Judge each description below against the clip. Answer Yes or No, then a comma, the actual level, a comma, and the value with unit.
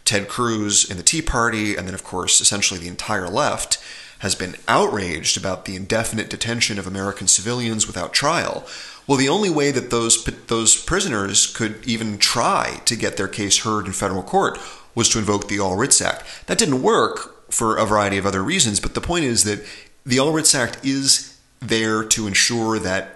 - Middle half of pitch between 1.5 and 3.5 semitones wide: Yes, average, 2.9 semitones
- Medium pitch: No, low, 110 Hz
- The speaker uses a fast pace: No, average, 195 wpm